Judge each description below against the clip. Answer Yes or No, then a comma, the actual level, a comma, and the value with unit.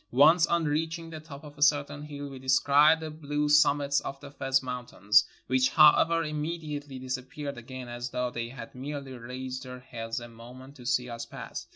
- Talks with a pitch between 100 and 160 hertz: Yes, medium, 140 Hz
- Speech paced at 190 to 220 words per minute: Yes, average, 195 wpm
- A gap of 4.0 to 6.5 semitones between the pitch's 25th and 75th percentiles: No, average, 2.9 semitones